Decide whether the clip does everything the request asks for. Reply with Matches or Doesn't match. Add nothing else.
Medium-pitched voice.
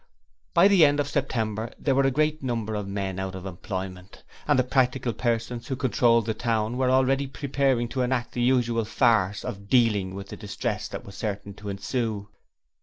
Doesn't match